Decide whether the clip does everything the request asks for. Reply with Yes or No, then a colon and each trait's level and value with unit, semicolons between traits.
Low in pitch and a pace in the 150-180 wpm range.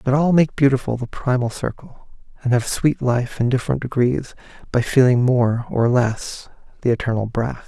Yes: low, 125 Hz; average, 170 wpm